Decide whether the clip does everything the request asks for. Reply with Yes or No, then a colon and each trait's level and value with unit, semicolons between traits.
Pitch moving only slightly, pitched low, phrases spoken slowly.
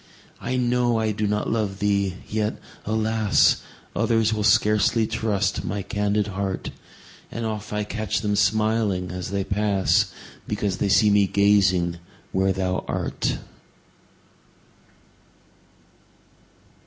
Yes: narrow, 1.8 semitones; low, 105 Hz; slow, 115 wpm